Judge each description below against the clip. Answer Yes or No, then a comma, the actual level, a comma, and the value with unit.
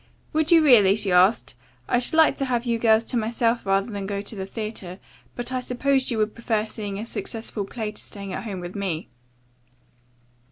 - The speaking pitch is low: No, high, 220 Hz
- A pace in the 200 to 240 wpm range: Yes, fast, 205 wpm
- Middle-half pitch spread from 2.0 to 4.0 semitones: Yes, average, 3.5 semitones